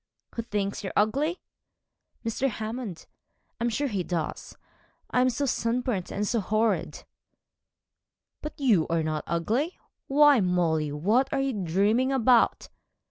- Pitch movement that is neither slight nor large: No, wide, 5.8 semitones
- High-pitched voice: Yes, high, 220 Hz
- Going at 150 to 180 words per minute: No, slow, 135 wpm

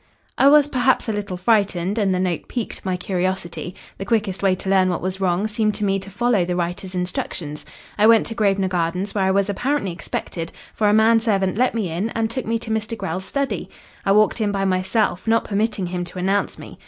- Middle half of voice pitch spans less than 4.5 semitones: Yes, average, 3.1 semitones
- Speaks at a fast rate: Yes, fast, 225 wpm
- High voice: Yes, high, 195 Hz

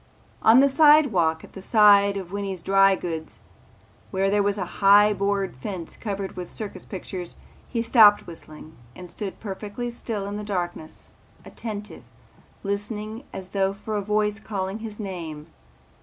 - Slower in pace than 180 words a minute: Yes, average, 155 wpm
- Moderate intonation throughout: No, narrow, 2.0 semitones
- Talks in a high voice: Yes, high, 200 Hz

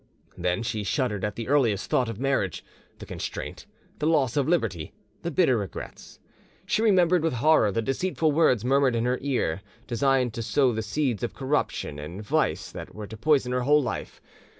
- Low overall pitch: Yes, low, 125 Hz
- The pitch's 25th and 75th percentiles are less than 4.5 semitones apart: No, average, 5.3 semitones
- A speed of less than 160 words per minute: No, average, 185 wpm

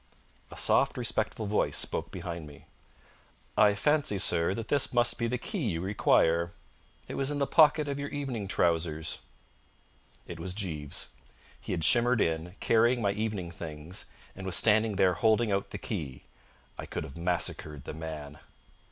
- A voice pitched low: Yes, very low, 95 Hz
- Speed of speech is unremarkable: Yes, average, 165 wpm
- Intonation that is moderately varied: No, wide, 6.1 semitones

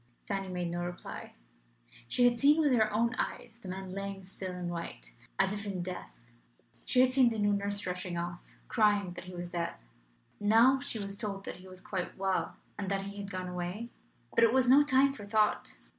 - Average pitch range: Yes, average, 3.9 semitones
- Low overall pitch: No, high, 200 Hz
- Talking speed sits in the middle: No, fast, 210 wpm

